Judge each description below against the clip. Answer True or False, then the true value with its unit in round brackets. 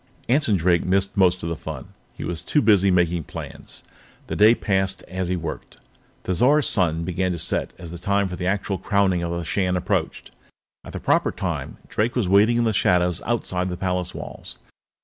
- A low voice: True (90 Hz)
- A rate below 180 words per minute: False (195 wpm)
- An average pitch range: False (2.3 semitones)